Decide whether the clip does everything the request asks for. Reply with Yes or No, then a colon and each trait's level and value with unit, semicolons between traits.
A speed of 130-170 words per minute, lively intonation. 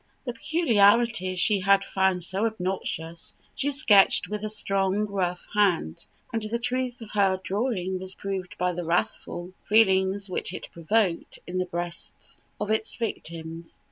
No: average, 150 wpm; average, 3.2 semitones